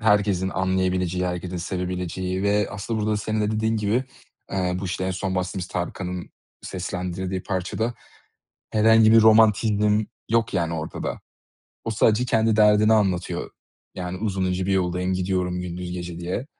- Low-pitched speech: Yes, very low, 95 Hz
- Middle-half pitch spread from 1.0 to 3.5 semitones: Yes, average, 2.8 semitones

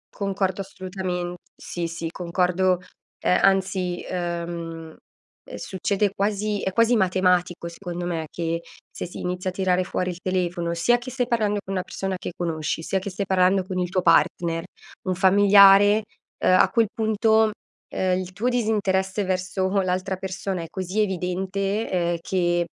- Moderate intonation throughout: No, narrow, 1.9 semitones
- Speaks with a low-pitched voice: No, medium, 185 Hz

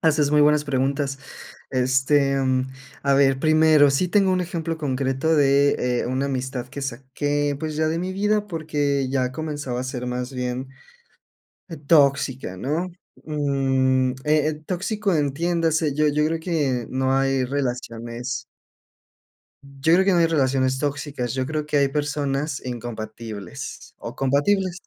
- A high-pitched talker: No, medium, 140 Hz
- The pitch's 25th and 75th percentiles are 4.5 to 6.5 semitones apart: No, average, 3.0 semitones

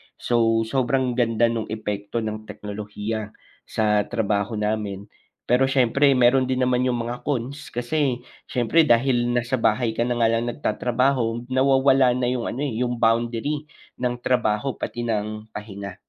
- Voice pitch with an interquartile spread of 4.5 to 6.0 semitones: No, average, 2.7 semitones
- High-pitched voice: No, low, 120 Hz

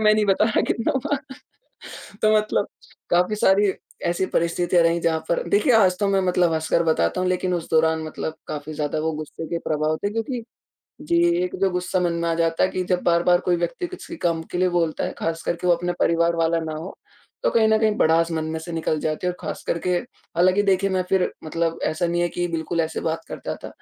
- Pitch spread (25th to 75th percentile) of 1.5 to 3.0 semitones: Yes, narrow, 2.6 semitones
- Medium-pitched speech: Yes, medium, 175 Hz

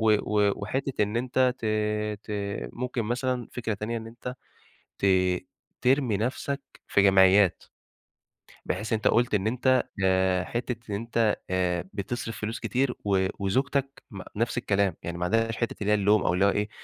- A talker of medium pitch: No, low, 110 Hz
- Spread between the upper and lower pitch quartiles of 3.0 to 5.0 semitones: Yes, average, 3.6 semitones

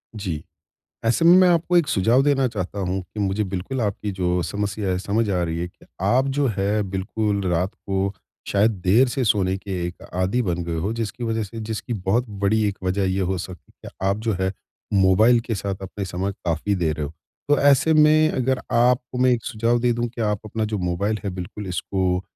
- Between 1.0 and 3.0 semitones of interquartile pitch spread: No, average, 4.0 semitones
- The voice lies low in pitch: Yes, low, 105 Hz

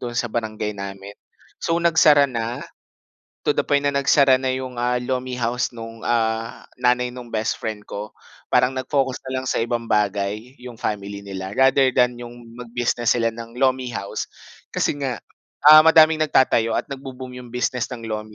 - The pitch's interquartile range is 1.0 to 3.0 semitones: Yes, narrow, 2.6 semitones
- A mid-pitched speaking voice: No, low, 125 Hz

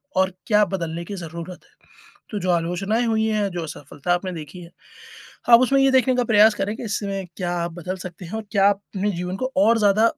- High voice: Yes, high, 195 Hz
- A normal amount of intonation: Yes, average, 3.8 semitones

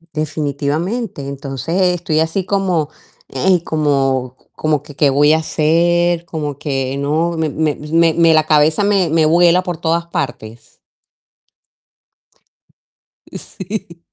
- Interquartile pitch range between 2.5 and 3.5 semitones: Yes, average, 2.9 semitones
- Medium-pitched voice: Yes, medium, 160 Hz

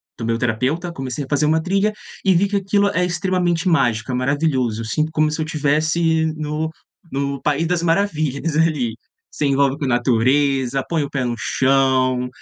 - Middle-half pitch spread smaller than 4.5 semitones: Yes, average, 4.0 semitones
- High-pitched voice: No, medium, 150 Hz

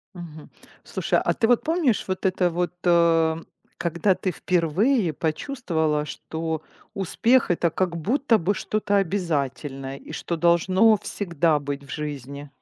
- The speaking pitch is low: No, medium, 170 Hz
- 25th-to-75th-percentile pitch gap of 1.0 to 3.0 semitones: No, average, 4.3 semitones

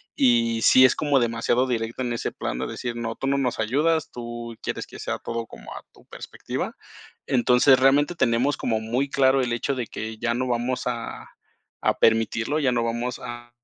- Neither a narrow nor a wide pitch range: No, narrow, 2.1 semitones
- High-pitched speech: No, low, 120 Hz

